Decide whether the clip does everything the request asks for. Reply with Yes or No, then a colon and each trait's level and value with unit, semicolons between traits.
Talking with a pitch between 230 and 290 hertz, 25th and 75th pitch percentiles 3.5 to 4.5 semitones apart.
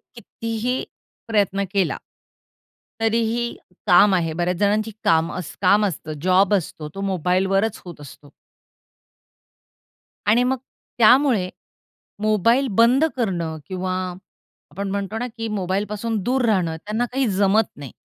No: high, 200 Hz; average, 3.8 semitones